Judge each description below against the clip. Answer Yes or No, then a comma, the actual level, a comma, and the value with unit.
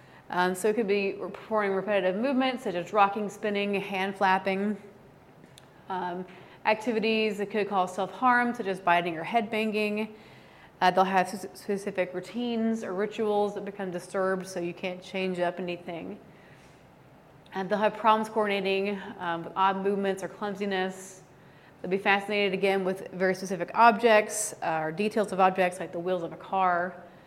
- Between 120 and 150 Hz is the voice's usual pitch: No, high, 195 Hz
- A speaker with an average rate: Yes, average, 160 wpm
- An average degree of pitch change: No, narrow, 2.3 semitones